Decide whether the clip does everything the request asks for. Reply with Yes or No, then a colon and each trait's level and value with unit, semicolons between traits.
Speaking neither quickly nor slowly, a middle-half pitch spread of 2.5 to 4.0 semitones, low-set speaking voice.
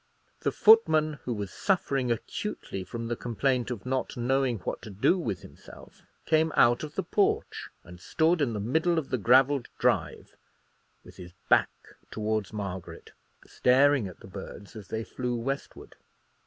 No: average, 160 wpm; average, 5.3 semitones; low, 125 Hz